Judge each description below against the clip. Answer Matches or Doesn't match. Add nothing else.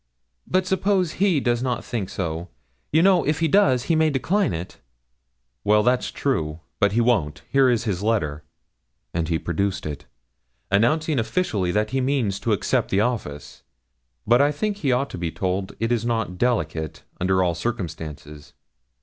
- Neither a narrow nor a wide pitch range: Doesn't match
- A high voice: Doesn't match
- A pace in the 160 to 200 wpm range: Matches